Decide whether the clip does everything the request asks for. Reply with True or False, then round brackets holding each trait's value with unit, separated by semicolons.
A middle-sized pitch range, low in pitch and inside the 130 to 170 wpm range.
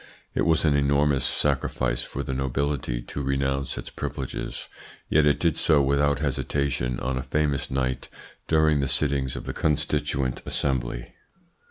False (1.8 semitones; 70 Hz; 150 wpm)